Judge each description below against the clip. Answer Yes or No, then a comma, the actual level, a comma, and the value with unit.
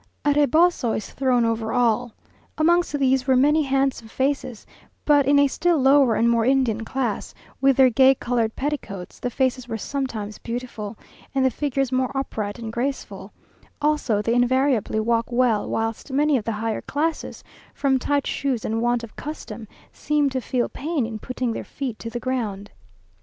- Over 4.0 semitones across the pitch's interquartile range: No, average, 3.4 semitones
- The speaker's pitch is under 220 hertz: No, very high, 255 Hz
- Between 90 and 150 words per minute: No, average, 175 wpm